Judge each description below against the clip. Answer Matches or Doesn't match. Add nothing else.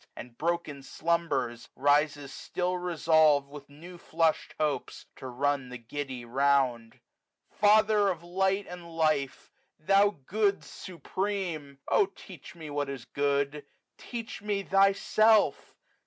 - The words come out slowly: Matches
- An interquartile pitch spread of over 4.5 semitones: Matches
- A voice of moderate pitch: Matches